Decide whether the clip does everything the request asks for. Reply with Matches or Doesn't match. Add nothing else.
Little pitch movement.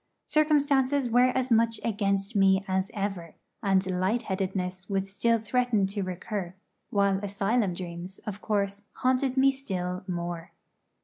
Doesn't match